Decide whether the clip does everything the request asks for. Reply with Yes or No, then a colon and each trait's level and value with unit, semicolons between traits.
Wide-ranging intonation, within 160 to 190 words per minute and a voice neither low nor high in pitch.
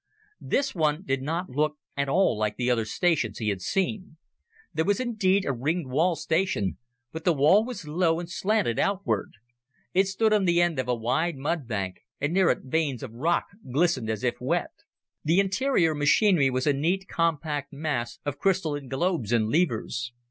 Yes: wide, 5.9 semitones; average, 180 wpm; medium, 155 Hz